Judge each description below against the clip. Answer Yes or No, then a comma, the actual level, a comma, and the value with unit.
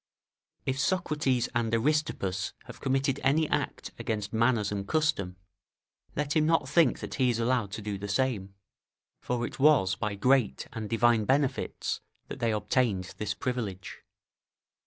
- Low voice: Yes, low, 120 Hz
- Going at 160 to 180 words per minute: No, average, 150 wpm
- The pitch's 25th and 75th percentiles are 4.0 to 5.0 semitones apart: Yes, average, 4.6 semitones